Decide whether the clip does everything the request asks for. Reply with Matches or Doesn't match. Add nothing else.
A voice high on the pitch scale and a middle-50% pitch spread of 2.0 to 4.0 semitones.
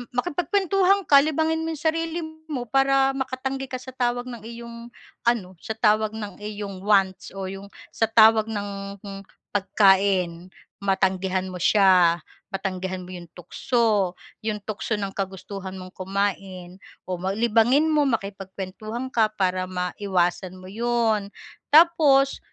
Doesn't match